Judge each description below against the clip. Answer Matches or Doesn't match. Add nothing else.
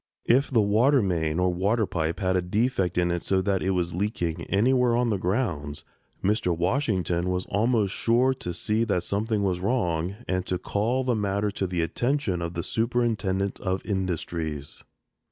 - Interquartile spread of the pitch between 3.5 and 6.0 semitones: Matches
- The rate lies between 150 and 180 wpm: Matches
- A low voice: Matches